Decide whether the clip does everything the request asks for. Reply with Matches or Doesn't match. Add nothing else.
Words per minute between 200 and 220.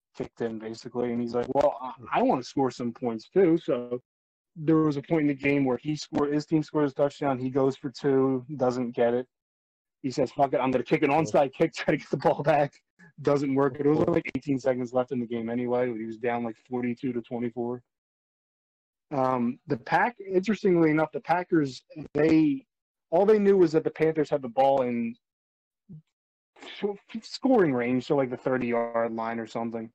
Matches